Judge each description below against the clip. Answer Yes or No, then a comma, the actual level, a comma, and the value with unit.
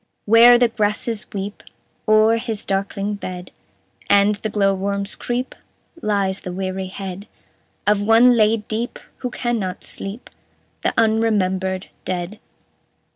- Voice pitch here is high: Yes, high, 205 Hz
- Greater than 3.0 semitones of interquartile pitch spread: No, average, 2.7 semitones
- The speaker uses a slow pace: Yes, slow, 125 wpm